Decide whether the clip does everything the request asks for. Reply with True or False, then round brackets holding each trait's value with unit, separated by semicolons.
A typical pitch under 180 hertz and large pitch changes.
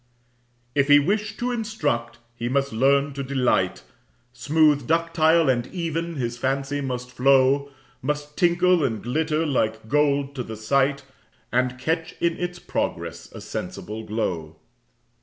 False (140 Hz; 4.4 semitones)